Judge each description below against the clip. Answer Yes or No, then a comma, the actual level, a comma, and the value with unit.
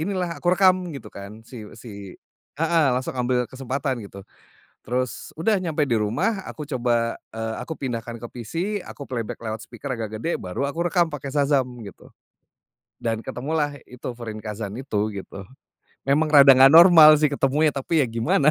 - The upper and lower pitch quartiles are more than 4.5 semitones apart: Yes, average, 5.1 semitones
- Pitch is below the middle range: Yes, low, 130 Hz